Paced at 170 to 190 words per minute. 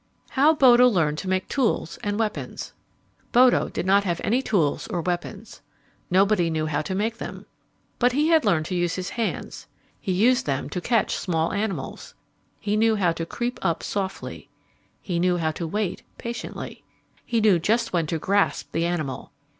Yes: average, 180 wpm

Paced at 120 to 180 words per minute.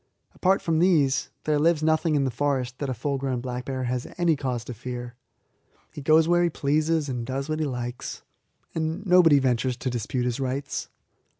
No: average, 195 wpm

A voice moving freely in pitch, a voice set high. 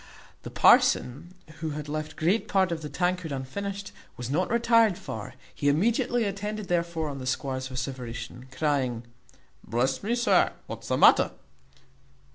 No: wide, 7.2 semitones; medium, 155 Hz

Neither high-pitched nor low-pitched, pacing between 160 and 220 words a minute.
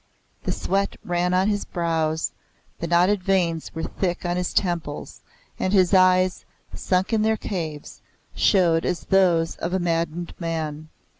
No: medium, 175 Hz; average, 150 wpm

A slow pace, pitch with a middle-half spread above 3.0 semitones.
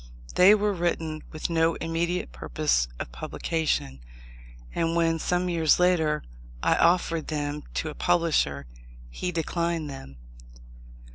No: slow, 125 wpm; narrow, 2.4 semitones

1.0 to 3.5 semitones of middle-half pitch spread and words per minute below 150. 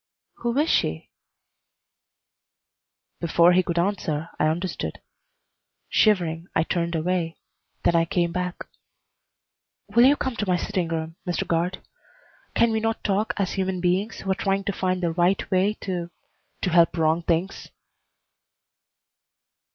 Yes: narrow, 2.6 semitones; average, 140 wpm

